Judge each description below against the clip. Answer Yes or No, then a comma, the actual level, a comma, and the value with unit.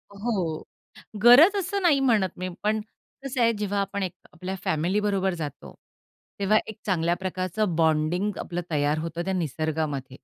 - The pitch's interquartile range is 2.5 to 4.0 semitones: No, average, 4.7 semitones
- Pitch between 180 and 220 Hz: Yes, medium, 185 Hz